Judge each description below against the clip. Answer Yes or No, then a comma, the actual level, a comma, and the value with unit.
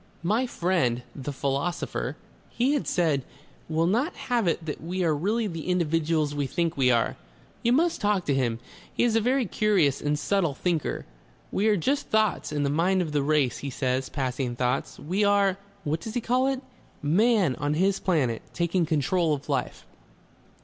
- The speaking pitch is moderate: Yes, medium, 170 Hz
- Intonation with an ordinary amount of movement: No, wide, 6.1 semitones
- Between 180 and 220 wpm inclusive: Yes, average, 185 wpm